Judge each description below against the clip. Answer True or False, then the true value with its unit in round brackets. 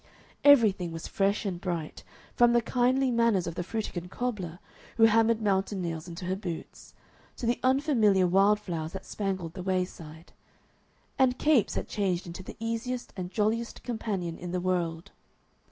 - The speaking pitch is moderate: False (195 Hz)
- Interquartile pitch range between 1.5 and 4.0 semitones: False (4.5 semitones)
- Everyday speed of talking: True (160 wpm)